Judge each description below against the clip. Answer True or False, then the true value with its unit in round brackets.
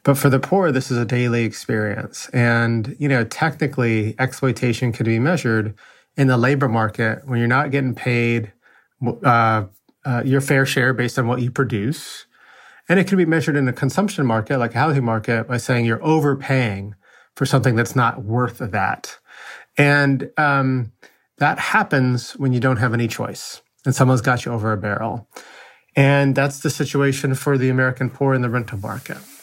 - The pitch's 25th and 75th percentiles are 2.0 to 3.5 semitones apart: True (2.9 semitones)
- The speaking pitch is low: True (130 Hz)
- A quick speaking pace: False (180 wpm)